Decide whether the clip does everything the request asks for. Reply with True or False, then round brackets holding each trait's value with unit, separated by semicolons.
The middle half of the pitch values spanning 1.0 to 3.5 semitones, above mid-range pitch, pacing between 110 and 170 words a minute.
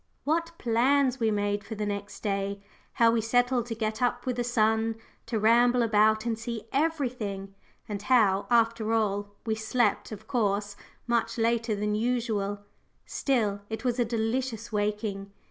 True (2.6 semitones; 225 Hz; 160 wpm)